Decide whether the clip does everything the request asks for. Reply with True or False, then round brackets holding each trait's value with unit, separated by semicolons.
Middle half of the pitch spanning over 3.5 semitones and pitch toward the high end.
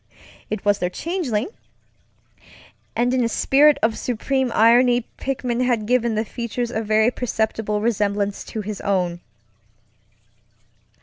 False (2.9 semitones; 230 Hz)